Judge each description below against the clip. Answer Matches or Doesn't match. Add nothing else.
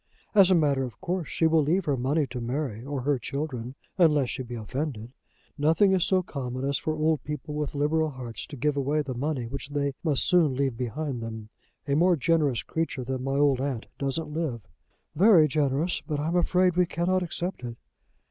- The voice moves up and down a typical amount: Matches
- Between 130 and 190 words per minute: Doesn't match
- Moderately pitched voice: Matches